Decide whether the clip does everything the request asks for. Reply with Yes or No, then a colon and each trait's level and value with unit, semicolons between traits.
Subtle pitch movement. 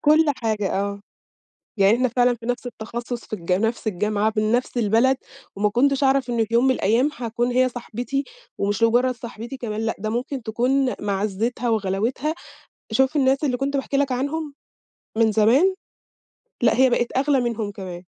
No: average, 3.4 semitones